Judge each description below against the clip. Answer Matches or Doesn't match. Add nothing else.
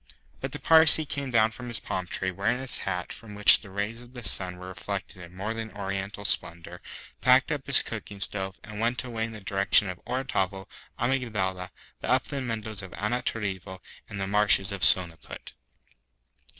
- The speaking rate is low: Doesn't match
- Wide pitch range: Doesn't match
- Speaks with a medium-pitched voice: Doesn't match